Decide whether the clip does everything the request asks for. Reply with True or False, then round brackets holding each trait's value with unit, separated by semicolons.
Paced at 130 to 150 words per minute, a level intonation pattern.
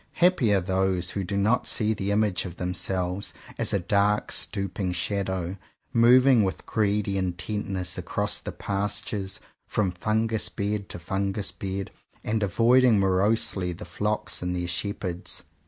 True (140 wpm; 2.3 semitones)